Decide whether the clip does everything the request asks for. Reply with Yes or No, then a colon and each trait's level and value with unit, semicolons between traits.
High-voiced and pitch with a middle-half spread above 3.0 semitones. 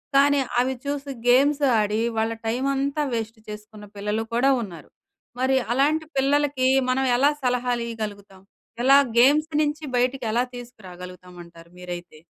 Yes: high, 245 Hz; average, 4.7 semitones